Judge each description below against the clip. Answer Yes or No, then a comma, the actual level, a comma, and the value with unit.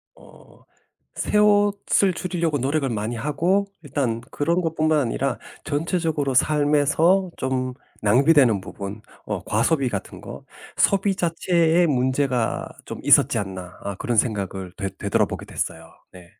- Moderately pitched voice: Yes, medium, 145 Hz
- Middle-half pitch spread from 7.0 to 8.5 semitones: No, wide, 6.6 semitones